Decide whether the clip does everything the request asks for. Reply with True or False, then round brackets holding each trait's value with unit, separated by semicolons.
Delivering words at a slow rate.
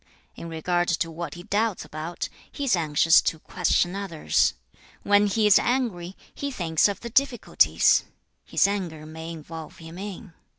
False (160 wpm)